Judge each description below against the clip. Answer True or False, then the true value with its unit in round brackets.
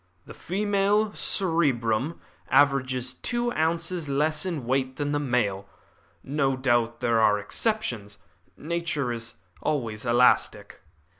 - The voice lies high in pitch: False (140 Hz)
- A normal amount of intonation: False (5.9 semitones)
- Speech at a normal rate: False (115 wpm)